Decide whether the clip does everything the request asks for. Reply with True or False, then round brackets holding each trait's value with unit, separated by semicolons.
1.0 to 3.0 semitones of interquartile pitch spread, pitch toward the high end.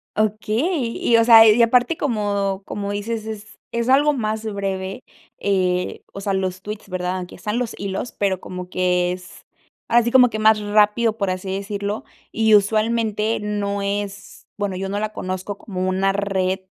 True (2.4 semitones; 205 Hz)